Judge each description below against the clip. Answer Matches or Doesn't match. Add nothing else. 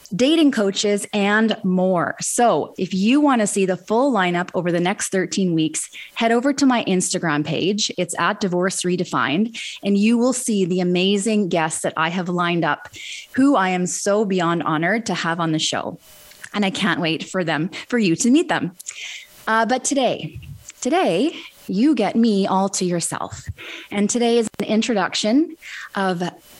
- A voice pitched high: Matches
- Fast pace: Doesn't match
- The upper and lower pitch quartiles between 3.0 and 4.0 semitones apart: Doesn't match